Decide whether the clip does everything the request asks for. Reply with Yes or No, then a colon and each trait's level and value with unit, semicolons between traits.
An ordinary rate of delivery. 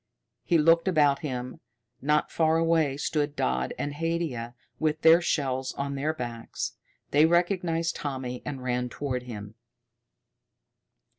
No: slow, 130 wpm